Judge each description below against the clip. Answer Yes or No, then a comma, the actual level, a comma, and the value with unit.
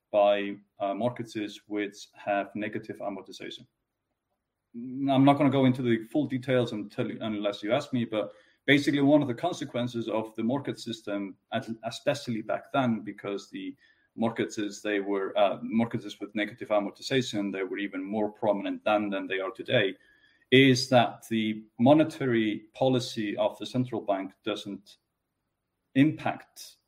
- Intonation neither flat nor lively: Yes, average, 3.8 semitones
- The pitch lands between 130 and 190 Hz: No, low, 110 Hz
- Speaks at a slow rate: No, average, 145 wpm